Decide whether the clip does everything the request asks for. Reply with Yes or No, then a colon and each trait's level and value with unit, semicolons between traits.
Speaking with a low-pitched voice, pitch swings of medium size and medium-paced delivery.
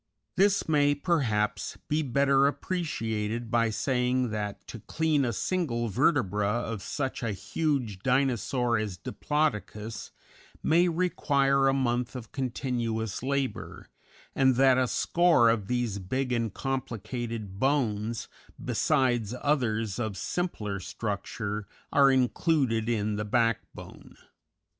No: low, 120 Hz; average, 4.2 semitones; slow, 115 wpm